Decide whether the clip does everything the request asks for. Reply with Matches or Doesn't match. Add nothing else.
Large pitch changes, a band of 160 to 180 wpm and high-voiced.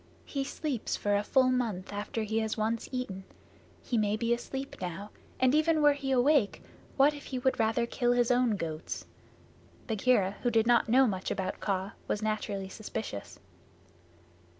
Doesn't match